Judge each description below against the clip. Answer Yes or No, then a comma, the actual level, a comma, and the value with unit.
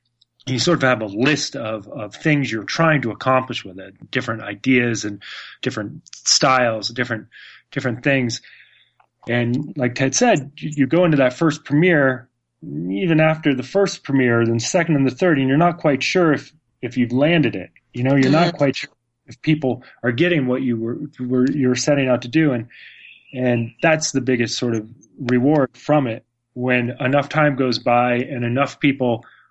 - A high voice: No, low, 130 Hz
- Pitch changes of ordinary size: Yes, average, 3.5 semitones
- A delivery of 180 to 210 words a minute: Yes, average, 185 wpm